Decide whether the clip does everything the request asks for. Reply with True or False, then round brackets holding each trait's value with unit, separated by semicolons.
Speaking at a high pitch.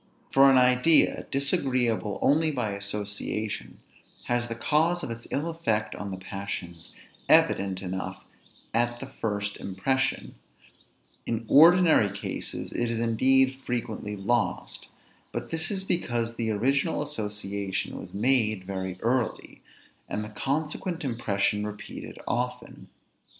False (115 Hz)